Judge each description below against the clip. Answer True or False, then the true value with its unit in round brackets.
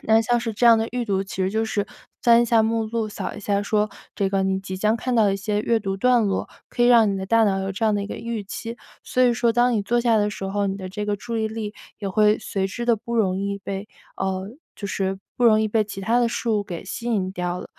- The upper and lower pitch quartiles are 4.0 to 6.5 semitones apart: False (2.8 semitones)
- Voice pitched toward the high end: True (210 Hz)